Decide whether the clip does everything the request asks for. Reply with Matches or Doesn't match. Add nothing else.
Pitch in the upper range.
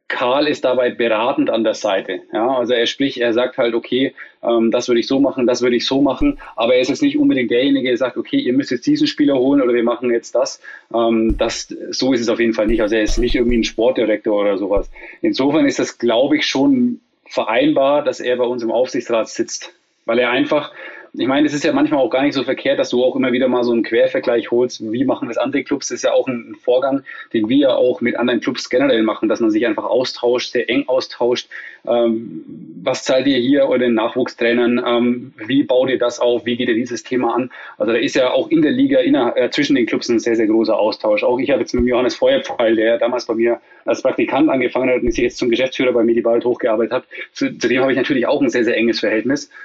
Doesn't match